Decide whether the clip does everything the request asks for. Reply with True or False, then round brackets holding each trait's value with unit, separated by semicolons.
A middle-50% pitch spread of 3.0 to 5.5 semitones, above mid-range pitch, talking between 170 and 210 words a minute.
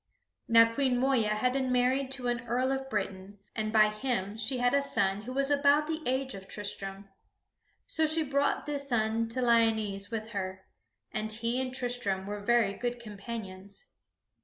True (4.0 semitones; 235 Hz; 175 wpm)